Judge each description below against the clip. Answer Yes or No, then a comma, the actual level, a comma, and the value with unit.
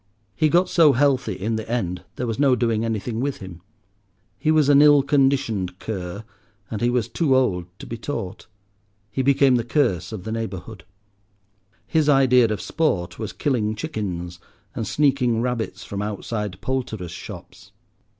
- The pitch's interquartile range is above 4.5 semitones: Yes, average, 4.9 semitones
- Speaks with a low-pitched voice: Yes, low, 115 Hz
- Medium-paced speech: Yes, average, 160 wpm